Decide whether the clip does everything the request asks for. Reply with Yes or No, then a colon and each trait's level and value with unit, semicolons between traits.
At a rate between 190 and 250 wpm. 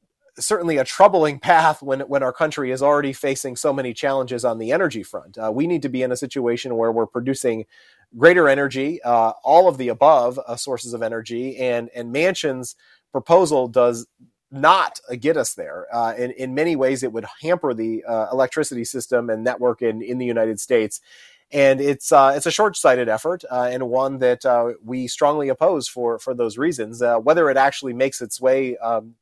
Yes: average, 200 wpm